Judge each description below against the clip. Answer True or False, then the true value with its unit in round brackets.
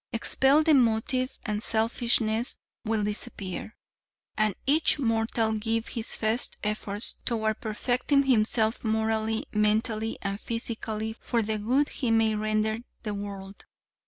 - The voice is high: True (220 Hz)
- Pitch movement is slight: True (1.7 semitones)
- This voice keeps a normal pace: False (125 wpm)